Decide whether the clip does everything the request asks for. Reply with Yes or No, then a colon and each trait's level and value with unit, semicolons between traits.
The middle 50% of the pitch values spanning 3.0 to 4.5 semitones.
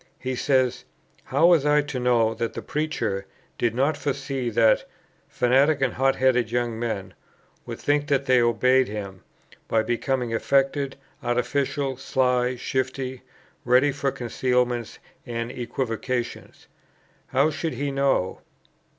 No: narrow, 2.5 semitones